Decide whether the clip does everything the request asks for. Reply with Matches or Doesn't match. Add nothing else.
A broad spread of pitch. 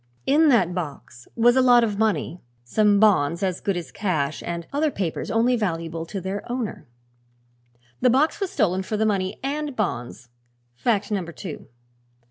Matches